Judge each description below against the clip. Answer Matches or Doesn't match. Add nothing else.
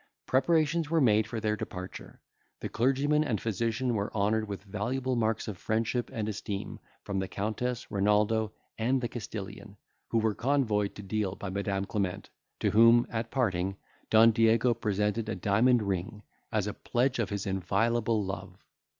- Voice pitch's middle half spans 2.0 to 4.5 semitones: Matches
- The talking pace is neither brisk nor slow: Matches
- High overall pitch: Doesn't match